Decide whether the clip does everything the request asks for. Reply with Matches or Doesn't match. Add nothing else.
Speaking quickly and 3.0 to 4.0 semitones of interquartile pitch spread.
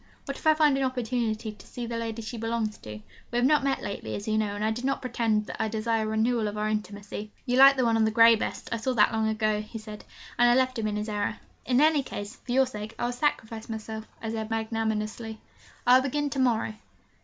Doesn't match